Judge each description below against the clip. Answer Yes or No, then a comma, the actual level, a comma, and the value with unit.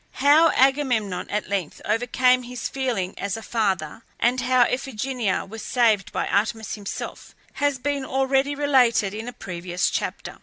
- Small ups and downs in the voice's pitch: No, average, 4.4 semitones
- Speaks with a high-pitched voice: Yes, high, 240 Hz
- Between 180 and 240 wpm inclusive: No, average, 150 wpm